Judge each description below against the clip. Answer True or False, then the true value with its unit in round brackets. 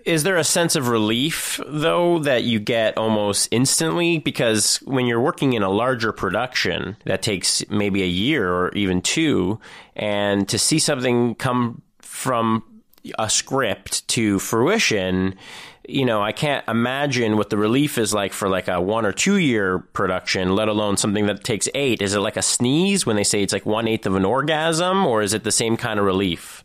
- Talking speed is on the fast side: False (190 wpm)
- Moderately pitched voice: False (110 Hz)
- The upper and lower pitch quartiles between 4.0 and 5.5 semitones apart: True (4.6 semitones)